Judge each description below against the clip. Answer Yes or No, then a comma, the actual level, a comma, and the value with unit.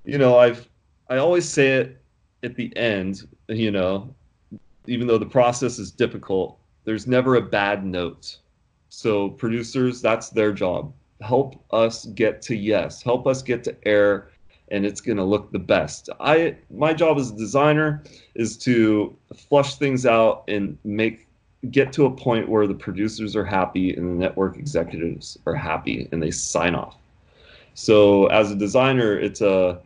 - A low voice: Yes, low, 110 Hz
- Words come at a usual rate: Yes, average, 165 wpm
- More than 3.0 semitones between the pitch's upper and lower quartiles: Yes, average, 4.0 semitones